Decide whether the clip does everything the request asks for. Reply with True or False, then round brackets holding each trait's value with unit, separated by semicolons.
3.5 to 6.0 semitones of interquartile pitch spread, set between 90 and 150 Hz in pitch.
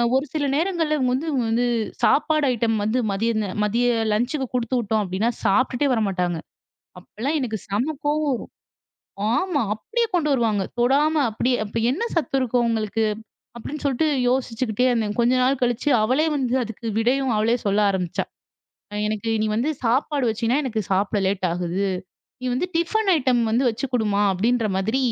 False (4.1 semitones; 240 Hz)